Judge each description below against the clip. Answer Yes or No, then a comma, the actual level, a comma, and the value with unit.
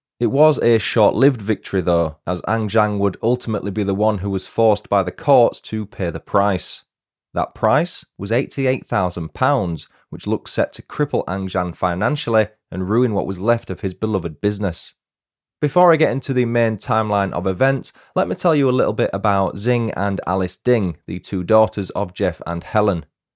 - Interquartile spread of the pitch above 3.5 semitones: Yes, average, 3.9 semitones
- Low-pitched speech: Yes, low, 105 Hz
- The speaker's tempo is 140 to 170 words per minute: No, average, 190 wpm